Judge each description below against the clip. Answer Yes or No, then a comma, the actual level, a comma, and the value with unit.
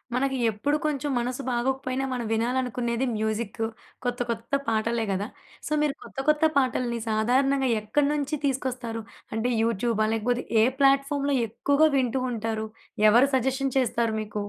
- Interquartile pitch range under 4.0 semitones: Yes, average, 3.1 semitones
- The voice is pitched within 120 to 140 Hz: No, high, 245 Hz